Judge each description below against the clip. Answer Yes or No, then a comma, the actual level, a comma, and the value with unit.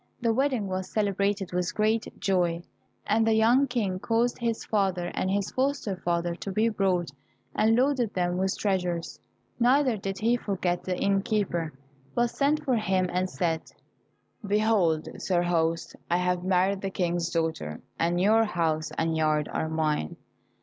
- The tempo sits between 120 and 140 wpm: No, average, 160 wpm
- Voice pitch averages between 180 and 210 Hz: Yes, high, 190 Hz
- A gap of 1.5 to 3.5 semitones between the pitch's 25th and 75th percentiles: No, average, 4.1 semitones